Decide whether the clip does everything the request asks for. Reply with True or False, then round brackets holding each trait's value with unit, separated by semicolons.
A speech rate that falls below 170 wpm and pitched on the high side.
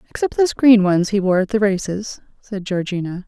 False (200 wpm; 200 Hz)